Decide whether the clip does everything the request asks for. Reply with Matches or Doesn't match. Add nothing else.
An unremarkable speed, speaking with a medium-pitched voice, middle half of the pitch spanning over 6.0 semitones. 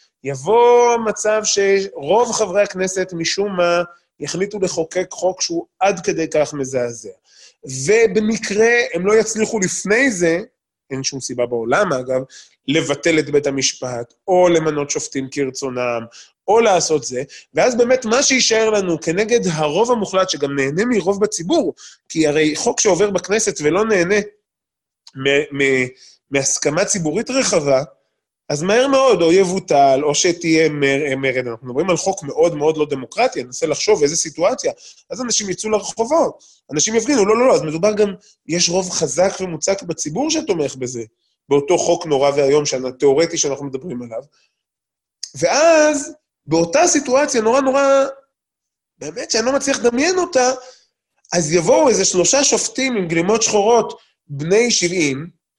Matches